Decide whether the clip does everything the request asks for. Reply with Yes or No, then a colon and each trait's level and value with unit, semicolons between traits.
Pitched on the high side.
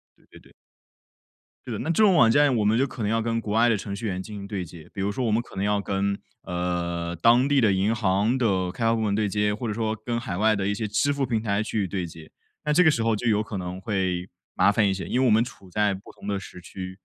No: low, 105 Hz